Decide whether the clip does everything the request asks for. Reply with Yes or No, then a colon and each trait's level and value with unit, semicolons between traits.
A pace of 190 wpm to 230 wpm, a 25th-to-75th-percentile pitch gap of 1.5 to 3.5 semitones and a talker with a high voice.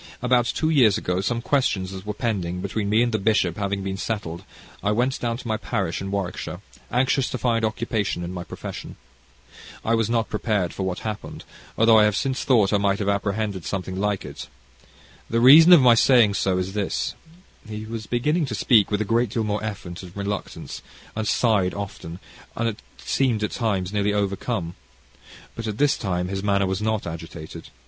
No: average, 195 wpm; average, 3.1 semitones; low, 105 Hz